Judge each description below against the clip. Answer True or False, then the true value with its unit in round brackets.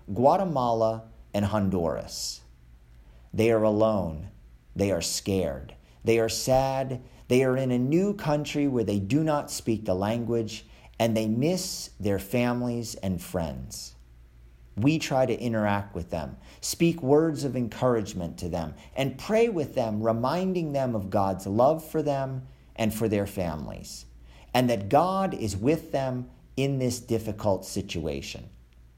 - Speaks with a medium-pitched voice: False (110 Hz)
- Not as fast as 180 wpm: True (145 wpm)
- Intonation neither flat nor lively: False (6.2 semitones)